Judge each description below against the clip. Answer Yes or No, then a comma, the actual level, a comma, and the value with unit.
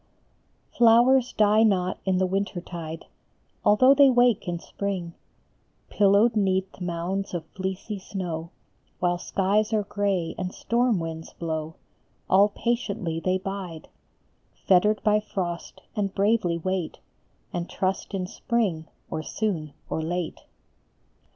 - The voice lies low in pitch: No, high, 190 Hz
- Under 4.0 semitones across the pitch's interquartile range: Yes, average, 3.3 semitones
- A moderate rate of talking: No, slow, 125 wpm